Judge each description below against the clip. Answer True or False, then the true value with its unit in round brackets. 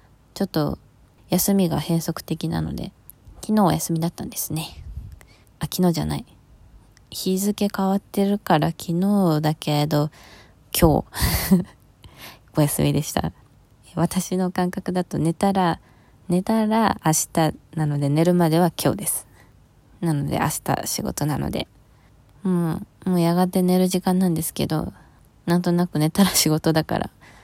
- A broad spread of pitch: False (4.3 semitones)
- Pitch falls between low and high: True (165 Hz)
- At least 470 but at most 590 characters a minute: False (260 characters per minute)